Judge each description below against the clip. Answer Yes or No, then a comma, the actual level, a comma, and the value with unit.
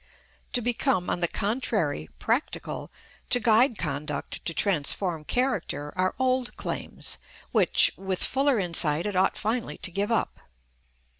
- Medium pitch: No, high, 200 Hz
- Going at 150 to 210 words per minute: No, slow, 135 wpm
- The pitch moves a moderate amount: No, wide, 6.4 semitones